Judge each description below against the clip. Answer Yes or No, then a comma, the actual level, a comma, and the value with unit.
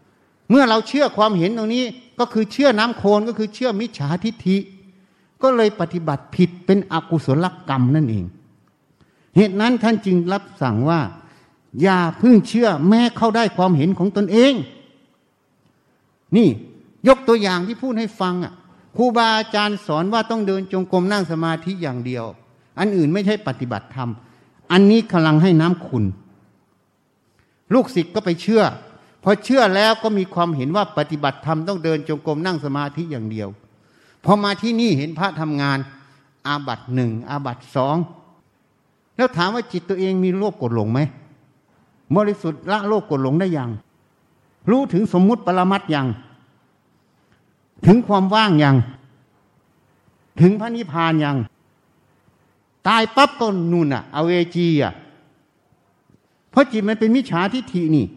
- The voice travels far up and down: Yes, wide, 6.4 semitones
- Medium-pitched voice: Yes, medium, 180 Hz